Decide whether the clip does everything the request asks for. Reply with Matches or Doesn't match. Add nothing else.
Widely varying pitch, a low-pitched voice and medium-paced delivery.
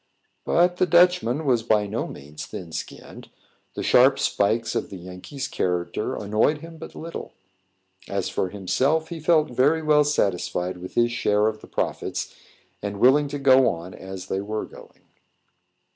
Matches